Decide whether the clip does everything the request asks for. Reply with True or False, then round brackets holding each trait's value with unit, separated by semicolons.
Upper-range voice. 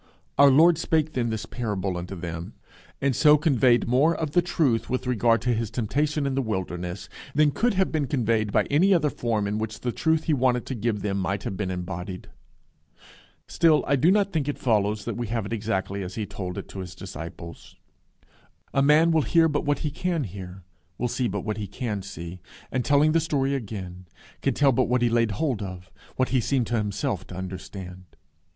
False (115 Hz)